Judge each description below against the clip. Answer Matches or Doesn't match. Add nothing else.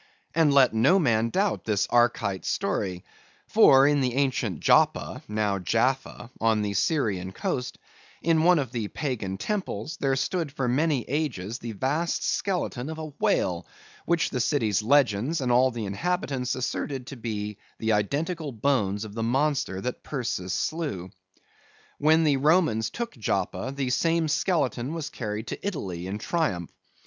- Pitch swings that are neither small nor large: Doesn't match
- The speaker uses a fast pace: Doesn't match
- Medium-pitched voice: Doesn't match